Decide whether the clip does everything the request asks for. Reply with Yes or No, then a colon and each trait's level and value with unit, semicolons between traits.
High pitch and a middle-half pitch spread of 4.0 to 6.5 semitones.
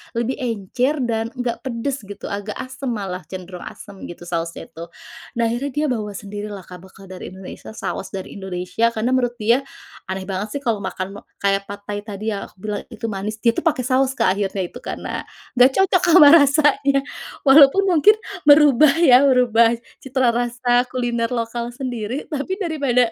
Yes: high, 235 Hz; average, 4.7 semitones